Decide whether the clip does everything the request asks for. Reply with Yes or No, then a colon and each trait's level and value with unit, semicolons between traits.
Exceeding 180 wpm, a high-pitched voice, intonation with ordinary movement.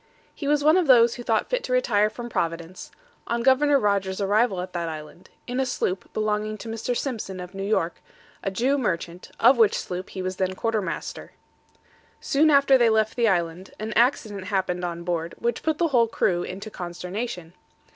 Yes: average, 195 wpm; high, 215 Hz; average, 4.9 semitones